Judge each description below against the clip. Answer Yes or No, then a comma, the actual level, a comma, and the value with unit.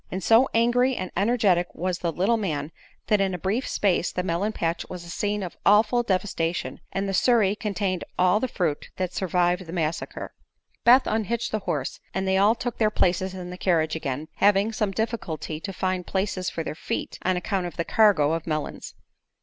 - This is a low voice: No, high, 190 Hz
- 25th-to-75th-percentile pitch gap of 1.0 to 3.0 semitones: No, average, 3.4 semitones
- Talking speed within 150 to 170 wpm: No, average, 200 wpm